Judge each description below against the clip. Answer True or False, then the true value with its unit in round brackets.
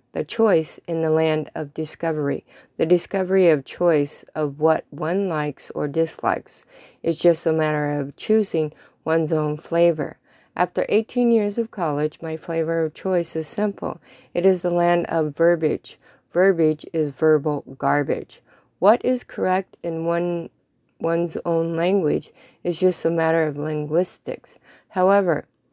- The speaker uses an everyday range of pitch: False (2.3 semitones)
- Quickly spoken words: False (140 wpm)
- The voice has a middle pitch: True (165 Hz)